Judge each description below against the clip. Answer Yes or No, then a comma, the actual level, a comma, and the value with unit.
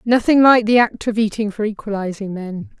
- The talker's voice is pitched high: Yes, high, 215 Hz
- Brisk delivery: No, average, 195 wpm